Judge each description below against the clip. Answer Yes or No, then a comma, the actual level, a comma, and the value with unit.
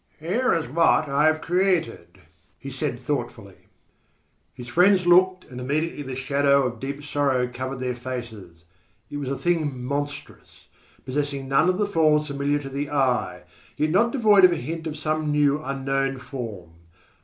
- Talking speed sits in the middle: Yes, average, 165 wpm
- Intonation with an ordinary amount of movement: Yes, average, 3.7 semitones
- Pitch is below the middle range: No, medium, 145 Hz